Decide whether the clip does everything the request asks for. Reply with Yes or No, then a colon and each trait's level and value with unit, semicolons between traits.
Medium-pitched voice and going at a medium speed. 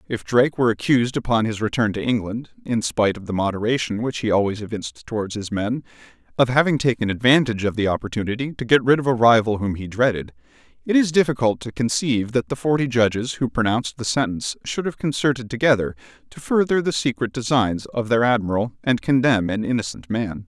No: low, 120 Hz; average, 190 wpm